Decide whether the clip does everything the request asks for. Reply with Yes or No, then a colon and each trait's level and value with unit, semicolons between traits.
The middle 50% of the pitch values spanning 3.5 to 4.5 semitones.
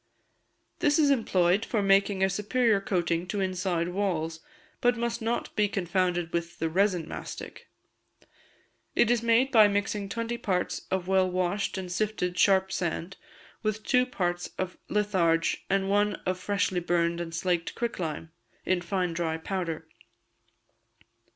No: average, 3.1 semitones